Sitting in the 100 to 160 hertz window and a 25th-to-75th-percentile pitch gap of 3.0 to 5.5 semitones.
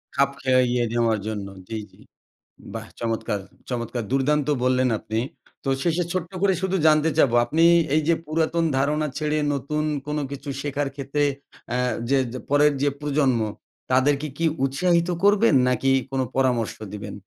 Yes: medium, 140 Hz; average, 3.5 semitones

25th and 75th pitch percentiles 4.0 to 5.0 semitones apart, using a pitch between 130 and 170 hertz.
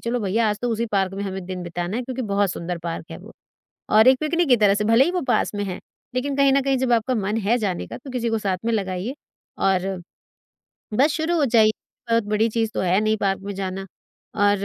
No: average, 4.3 semitones; high, 215 Hz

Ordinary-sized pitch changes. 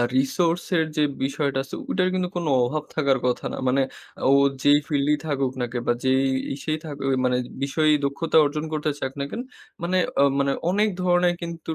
Yes: average, 3.6 semitones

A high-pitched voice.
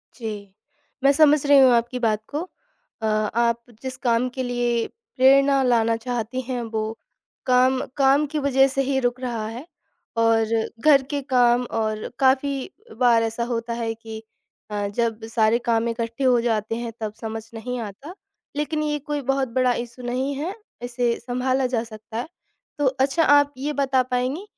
Yes: high, 245 Hz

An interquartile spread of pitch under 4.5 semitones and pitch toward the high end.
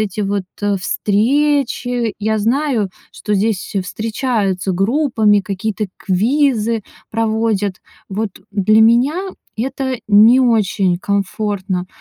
Yes: average, 3.3 semitones; high, 215 Hz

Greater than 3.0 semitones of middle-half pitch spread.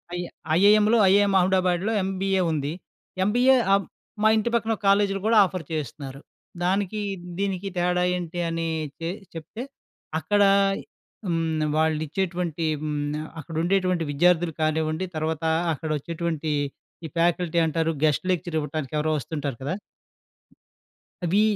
Yes: average, 3.6 semitones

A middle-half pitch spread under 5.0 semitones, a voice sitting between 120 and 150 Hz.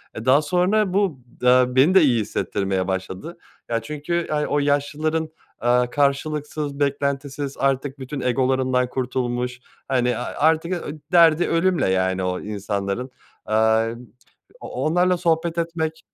Yes: average, 4.4 semitones; medium, 140 Hz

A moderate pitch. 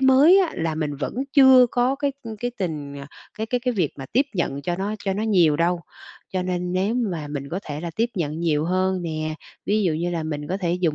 Yes: medium, 180 Hz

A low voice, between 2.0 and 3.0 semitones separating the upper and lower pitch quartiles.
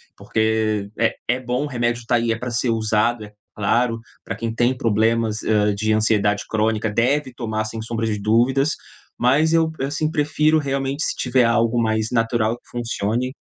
Yes: low, 115 Hz; narrow, 2.4 semitones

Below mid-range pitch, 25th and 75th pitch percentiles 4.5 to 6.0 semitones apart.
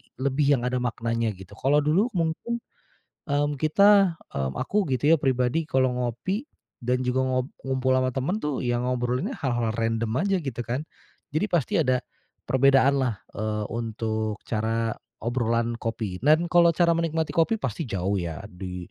Yes: low, 130 Hz; average, 5.1 semitones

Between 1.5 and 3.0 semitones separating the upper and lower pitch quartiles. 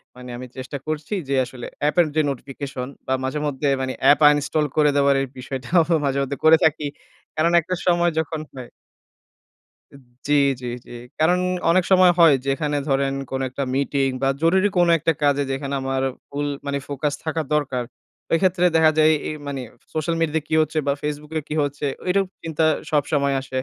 Yes: average, 2.7 semitones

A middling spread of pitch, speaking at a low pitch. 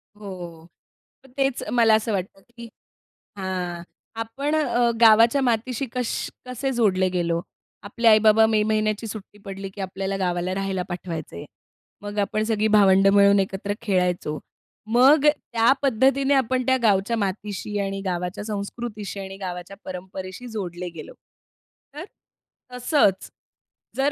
No: average, 3.8 semitones; high, 205 Hz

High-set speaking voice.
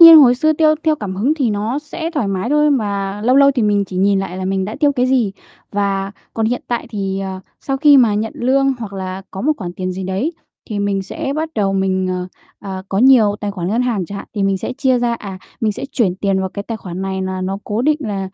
Yes: high, 205 Hz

